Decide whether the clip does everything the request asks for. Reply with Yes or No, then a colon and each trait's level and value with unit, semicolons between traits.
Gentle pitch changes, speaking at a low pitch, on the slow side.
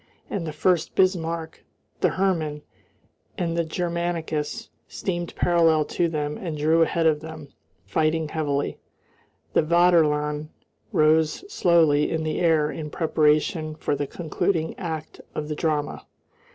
No: narrow, 2.0 semitones; medium, 160 Hz; slow, 130 wpm